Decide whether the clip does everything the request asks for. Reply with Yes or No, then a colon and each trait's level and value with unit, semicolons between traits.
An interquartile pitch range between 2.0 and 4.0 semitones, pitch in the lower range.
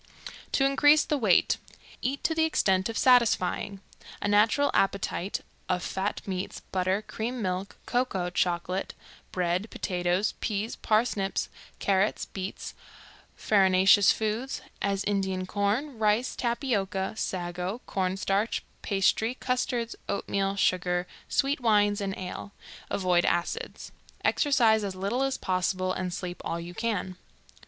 No: average, 3.7 semitones; high, 200 Hz